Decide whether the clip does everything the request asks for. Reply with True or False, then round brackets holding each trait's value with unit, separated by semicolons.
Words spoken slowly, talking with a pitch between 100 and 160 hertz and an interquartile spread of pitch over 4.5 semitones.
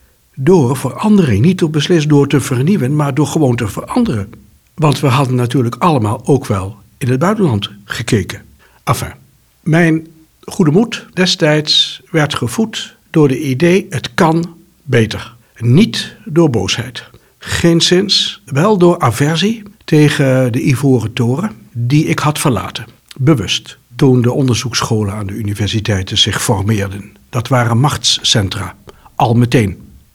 True (130 wpm; 140 Hz; 5.6 semitones)